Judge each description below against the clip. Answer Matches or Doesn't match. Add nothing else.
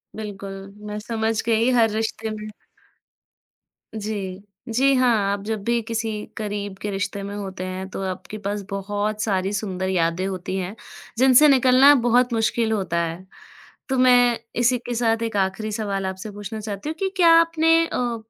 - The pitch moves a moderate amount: Matches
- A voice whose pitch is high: Matches